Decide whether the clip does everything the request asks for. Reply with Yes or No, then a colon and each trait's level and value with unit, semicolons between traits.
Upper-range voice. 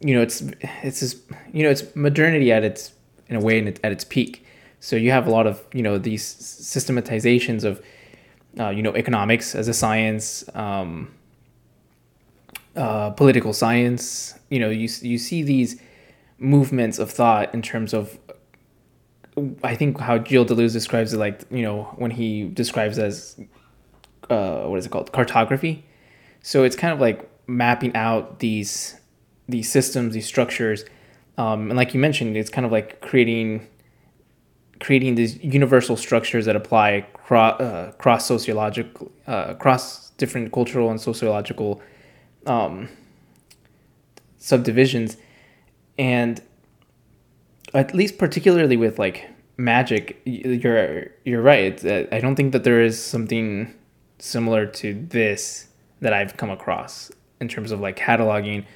No: low, 115 Hz